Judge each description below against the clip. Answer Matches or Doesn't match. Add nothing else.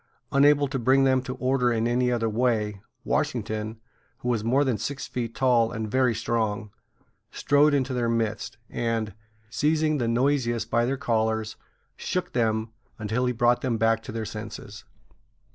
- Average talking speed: Matches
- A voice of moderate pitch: Doesn't match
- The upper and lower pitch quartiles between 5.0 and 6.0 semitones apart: Doesn't match